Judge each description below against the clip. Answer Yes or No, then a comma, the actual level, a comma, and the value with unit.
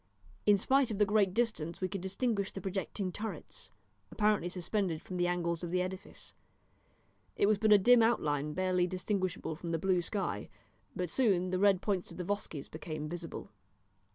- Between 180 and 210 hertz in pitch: Yes, medium, 185 Hz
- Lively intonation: No, average, 2.8 semitones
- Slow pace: No, average, 180 wpm